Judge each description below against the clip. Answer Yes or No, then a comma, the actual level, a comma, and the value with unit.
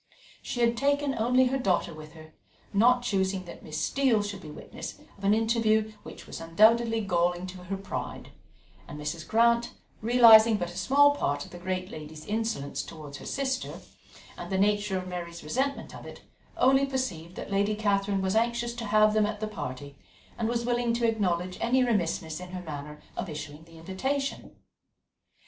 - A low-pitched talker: No, high, 205 Hz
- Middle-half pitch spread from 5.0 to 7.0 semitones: Yes, average, 5.3 semitones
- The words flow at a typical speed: Yes, average, 185 wpm